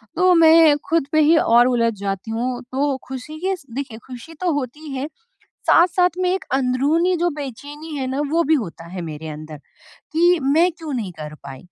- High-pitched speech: Yes, very high, 280 Hz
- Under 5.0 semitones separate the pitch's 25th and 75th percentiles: No, wide, 5.6 semitones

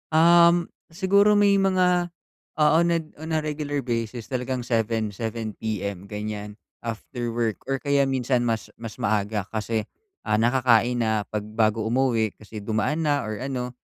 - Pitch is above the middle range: No, low, 120 Hz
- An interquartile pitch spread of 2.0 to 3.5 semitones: No, wide, 5.5 semitones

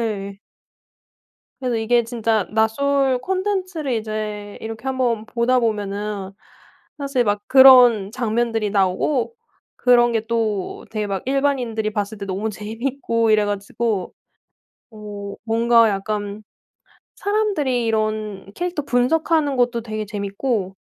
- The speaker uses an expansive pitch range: No, average, 3.3 semitones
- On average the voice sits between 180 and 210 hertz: No, high, 225 Hz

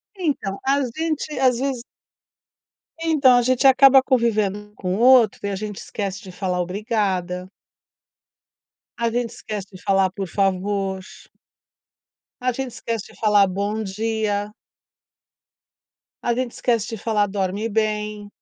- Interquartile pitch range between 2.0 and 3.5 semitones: No, average, 3.9 semitones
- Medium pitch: No, high, 215 Hz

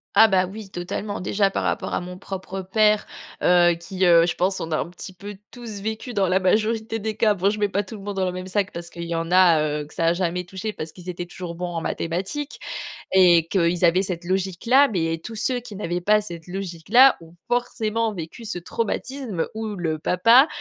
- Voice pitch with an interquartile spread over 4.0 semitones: No, average, 3.5 semitones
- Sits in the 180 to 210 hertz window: Yes, high, 190 Hz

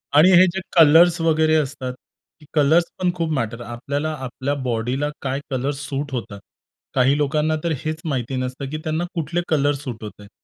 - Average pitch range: Yes, average, 3.5 semitones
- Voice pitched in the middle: Yes, medium, 145 Hz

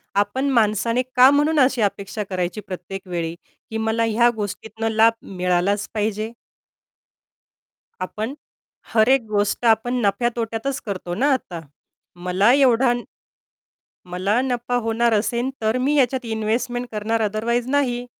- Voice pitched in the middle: No, high, 225 Hz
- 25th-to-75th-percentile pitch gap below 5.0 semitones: Yes, average, 3.2 semitones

